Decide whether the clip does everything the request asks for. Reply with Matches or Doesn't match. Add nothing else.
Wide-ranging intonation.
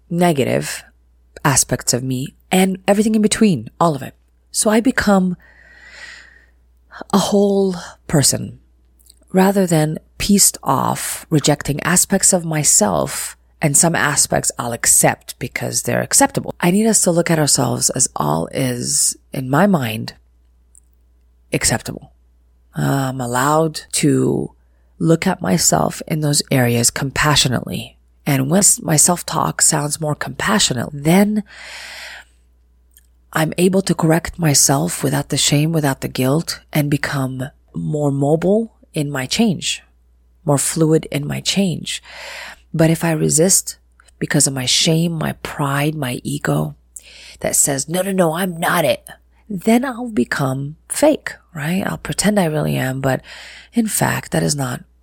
Matches